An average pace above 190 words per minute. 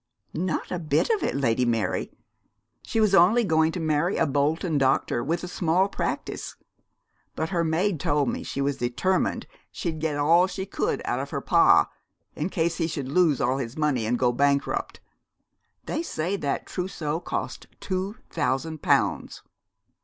No: average, 170 wpm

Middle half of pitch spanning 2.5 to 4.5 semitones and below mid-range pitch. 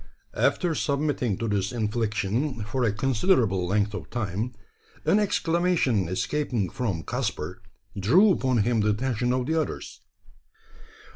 No: wide, 5.4 semitones; low, 120 Hz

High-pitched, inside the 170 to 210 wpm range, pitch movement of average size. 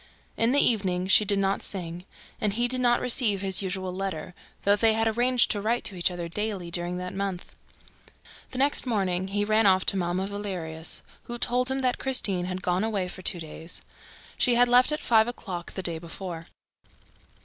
Yes: high, 195 Hz; average, 195 wpm; average, 4.0 semitones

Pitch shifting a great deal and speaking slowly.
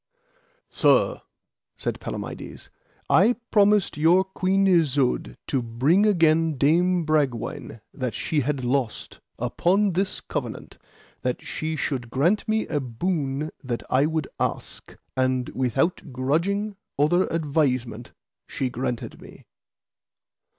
Yes: wide, 5.8 semitones; slow, 115 wpm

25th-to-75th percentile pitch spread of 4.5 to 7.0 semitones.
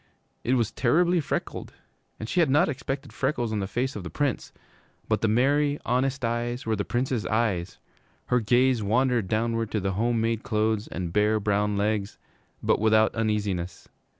No: average, 3.5 semitones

